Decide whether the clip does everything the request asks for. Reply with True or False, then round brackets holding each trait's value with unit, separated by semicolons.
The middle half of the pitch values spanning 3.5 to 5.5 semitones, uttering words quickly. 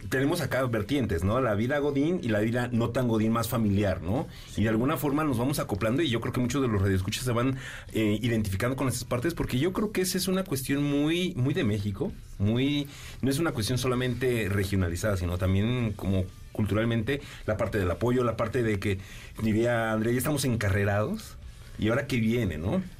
True (4.0 semitones; 205 wpm)